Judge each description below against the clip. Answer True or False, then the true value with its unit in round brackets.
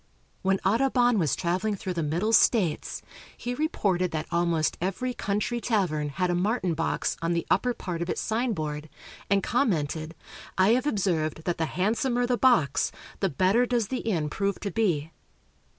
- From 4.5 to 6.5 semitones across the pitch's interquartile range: True (5.5 semitones)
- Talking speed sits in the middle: True (165 wpm)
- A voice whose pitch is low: False (190 Hz)